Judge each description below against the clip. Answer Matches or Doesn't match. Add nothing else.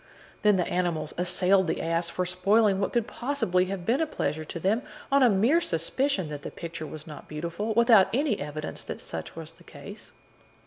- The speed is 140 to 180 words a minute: Doesn't match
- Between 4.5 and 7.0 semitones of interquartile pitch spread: Matches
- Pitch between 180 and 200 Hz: Matches